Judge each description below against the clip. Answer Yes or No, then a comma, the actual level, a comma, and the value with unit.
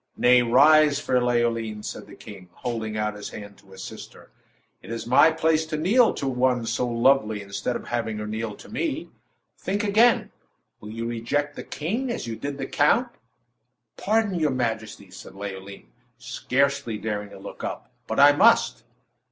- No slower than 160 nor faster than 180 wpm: Yes, average, 175 wpm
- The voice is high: No, low, 120 Hz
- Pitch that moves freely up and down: Yes, wide, 5.8 semitones